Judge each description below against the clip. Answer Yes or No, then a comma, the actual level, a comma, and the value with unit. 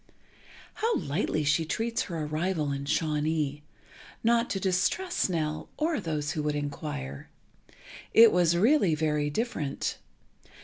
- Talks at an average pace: No, slow, 120 wpm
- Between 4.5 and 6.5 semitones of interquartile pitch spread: Yes, average, 5.1 semitones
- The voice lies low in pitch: No, medium, 160 Hz